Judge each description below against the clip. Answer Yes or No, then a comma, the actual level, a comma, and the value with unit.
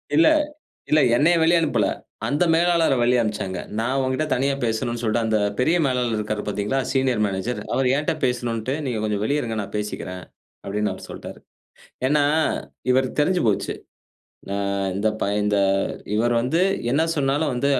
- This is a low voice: Yes, low, 125 Hz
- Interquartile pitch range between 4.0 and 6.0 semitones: Yes, average, 4.7 semitones